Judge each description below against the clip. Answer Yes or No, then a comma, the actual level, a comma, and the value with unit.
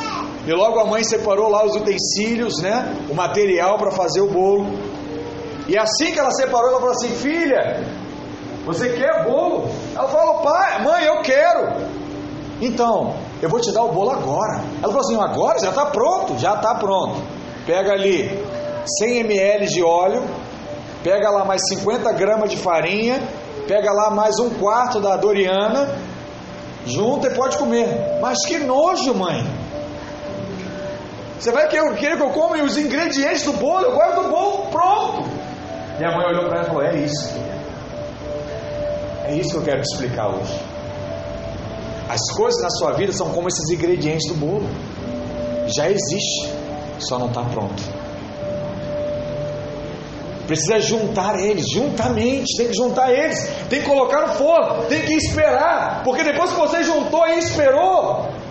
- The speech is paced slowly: No, average, 155 wpm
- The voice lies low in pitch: No, high, 210 Hz